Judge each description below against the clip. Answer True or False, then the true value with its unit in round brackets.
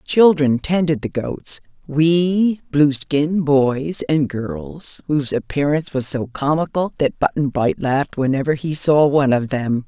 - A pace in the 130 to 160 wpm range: True (140 wpm)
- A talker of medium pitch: True (145 Hz)